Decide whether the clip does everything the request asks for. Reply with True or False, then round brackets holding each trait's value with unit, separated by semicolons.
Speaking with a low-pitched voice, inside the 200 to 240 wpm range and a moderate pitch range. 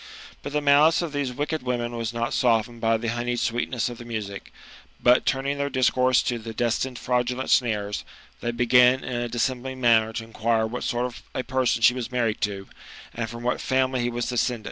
False (120 Hz; 205 wpm; 1.8 semitones)